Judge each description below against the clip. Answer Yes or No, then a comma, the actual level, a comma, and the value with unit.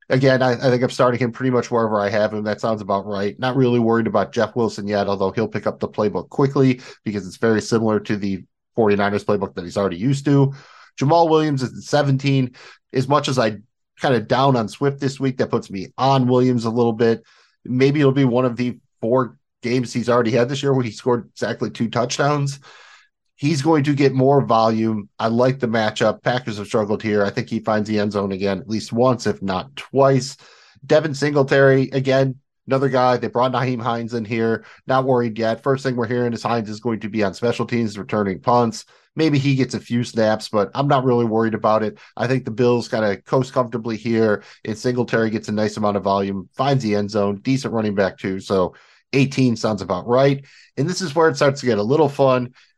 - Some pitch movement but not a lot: Yes, average, 3.6 semitones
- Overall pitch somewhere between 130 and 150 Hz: No, low, 120 Hz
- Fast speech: Yes, fast, 225 wpm